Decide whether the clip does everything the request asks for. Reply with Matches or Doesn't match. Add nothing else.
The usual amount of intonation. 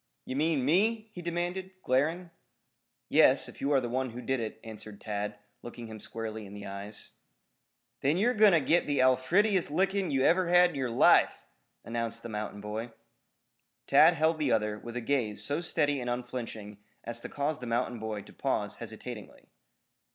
Doesn't match